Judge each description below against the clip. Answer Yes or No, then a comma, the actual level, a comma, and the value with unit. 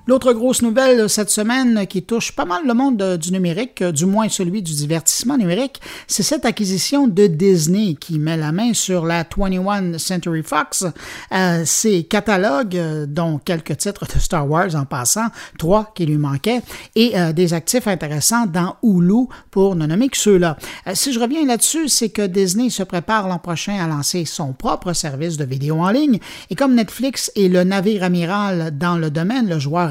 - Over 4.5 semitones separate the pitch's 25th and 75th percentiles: Yes, average, 5.1 semitones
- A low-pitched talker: No, high, 190 Hz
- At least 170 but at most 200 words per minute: Yes, average, 185 wpm